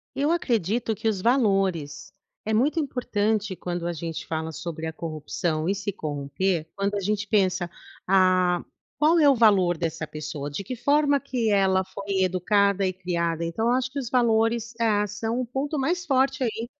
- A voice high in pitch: Yes, high, 200 Hz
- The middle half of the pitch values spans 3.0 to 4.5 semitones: No, average, 5.2 semitones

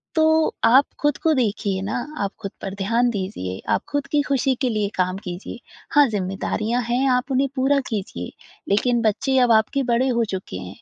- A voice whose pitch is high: Yes, high, 235 Hz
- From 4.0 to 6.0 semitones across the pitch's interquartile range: Yes, average, 5.3 semitones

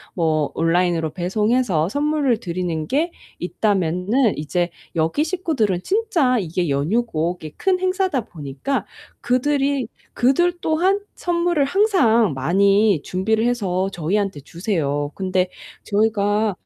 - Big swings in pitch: Yes, wide, 8.0 semitones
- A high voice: Yes, high, 205 Hz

